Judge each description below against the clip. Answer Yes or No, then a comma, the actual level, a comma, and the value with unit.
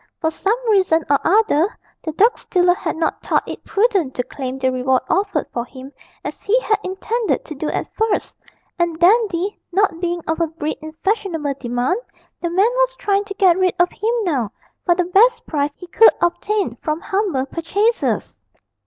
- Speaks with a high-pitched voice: Yes, very high, 355 Hz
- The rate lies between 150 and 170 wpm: No, average, 185 wpm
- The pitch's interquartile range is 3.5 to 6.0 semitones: Yes, average, 5.1 semitones